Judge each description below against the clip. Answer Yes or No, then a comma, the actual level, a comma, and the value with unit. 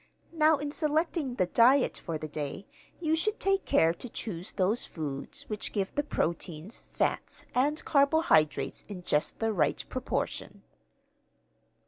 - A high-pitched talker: Yes, high, 230 Hz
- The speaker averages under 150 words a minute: Yes, average, 140 wpm